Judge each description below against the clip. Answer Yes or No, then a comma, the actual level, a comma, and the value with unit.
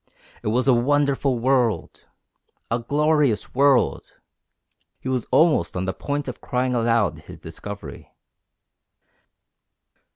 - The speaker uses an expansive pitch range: No, average, 3.7 semitones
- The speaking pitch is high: No, low, 125 Hz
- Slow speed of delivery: Yes, slow, 110 wpm